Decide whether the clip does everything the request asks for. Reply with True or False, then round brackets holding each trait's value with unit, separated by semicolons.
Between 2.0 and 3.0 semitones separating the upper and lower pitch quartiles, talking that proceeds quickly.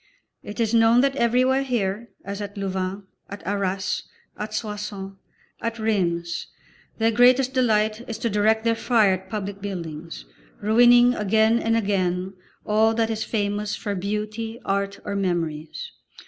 False (2.6 semitones; 145 wpm)